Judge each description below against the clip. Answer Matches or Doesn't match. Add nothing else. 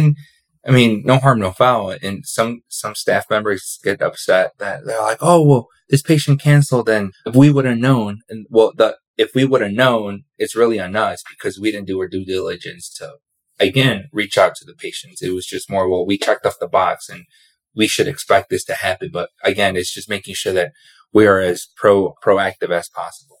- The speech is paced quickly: Matches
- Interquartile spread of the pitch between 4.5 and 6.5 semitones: Matches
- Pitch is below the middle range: Matches